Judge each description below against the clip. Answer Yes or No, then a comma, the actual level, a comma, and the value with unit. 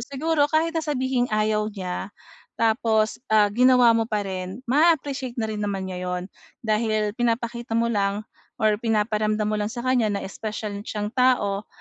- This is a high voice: Yes, high, 220 Hz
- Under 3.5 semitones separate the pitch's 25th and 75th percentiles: Yes, average, 2.9 semitones